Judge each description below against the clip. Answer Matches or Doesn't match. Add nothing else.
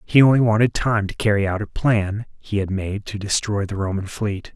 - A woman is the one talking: Doesn't match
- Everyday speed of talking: Doesn't match